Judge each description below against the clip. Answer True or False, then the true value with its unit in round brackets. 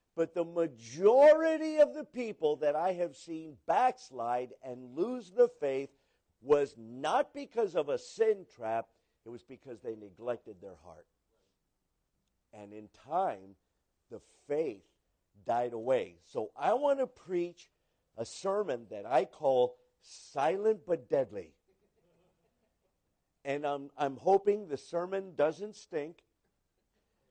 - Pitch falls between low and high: True (155 Hz)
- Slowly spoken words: True (125 wpm)